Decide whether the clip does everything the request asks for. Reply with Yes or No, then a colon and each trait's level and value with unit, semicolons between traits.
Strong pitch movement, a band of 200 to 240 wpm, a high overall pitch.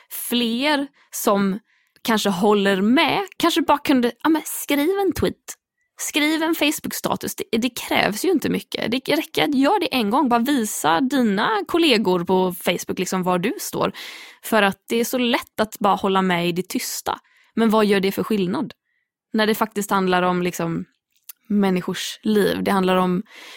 No: wide, 7.2 semitones; average, 175 wpm; high, 225 Hz